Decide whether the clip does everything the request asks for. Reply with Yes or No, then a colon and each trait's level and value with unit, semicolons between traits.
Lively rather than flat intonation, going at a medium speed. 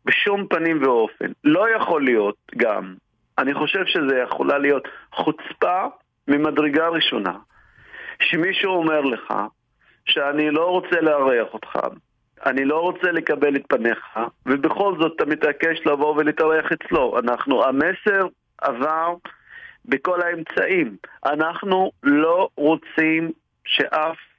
No: average, 3.7 semitones; average, 110 wpm